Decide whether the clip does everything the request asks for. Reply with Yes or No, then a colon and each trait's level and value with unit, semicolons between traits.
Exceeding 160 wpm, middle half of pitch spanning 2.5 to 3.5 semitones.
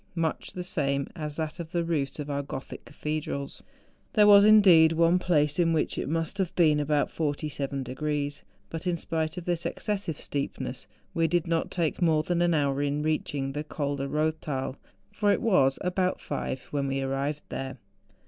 Yes: average, 185 wpm; average, 3.2 semitones